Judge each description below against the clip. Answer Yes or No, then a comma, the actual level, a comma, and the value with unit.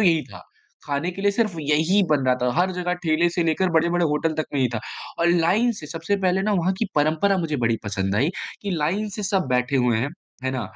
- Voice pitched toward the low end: No, medium, 165 Hz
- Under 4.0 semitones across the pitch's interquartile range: No, average, 4.7 semitones